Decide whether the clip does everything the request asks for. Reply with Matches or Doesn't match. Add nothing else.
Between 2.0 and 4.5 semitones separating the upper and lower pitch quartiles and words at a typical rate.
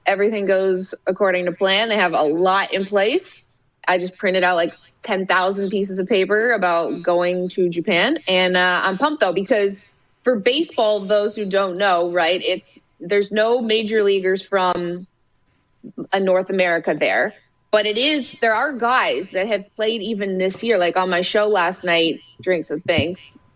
Matches